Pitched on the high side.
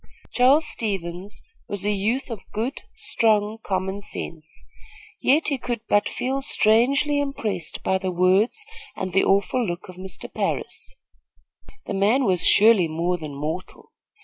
Yes: high, 205 Hz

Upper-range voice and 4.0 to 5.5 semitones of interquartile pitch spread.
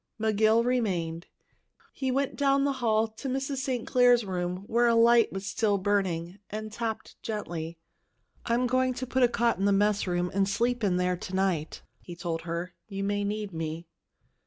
Yes: high, 210 Hz; average, 4.7 semitones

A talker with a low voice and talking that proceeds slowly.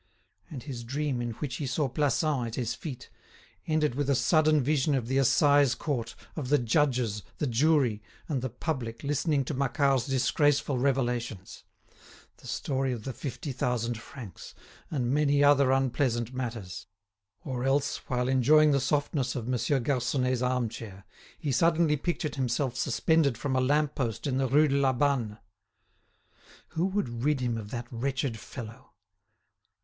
No: low, 130 Hz; average, 160 wpm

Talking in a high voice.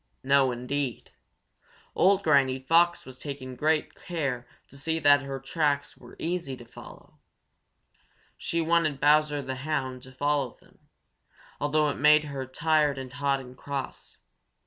No: medium, 140 Hz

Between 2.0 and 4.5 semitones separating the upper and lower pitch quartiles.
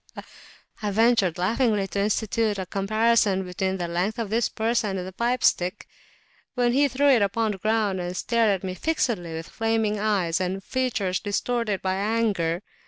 Yes: average, 3.5 semitones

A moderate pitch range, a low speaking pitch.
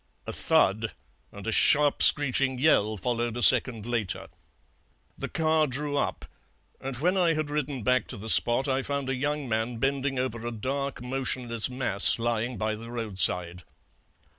Yes: average, 3.7 semitones; low, 125 Hz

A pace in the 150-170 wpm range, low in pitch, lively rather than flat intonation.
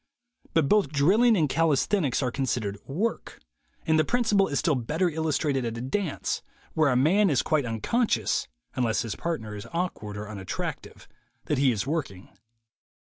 No: average, 165 wpm; medium, 145 Hz; wide, 6.2 semitones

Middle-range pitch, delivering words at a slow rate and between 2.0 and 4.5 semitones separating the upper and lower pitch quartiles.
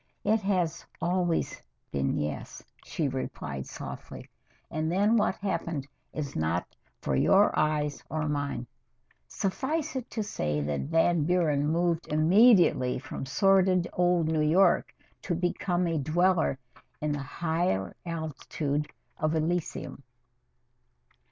Yes: medium, 160 Hz; slow, 120 wpm; average, 3.8 semitones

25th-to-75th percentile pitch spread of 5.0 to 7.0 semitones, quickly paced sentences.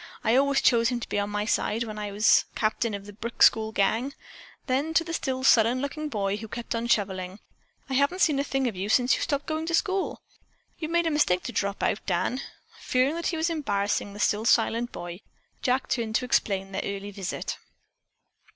Yes: average, 5.3 semitones; fast, 215 wpm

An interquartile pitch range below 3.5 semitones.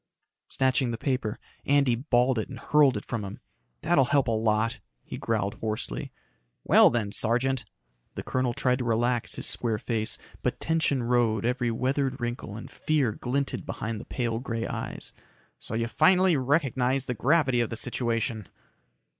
Yes: average, 2.7 semitones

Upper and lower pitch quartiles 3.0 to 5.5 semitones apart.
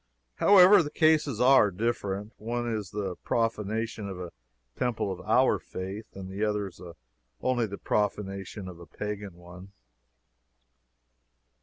Yes: average, 3.4 semitones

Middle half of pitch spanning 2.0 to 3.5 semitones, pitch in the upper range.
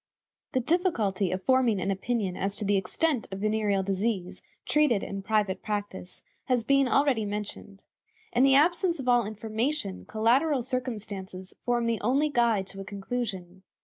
No: average, 4.5 semitones; high, 220 Hz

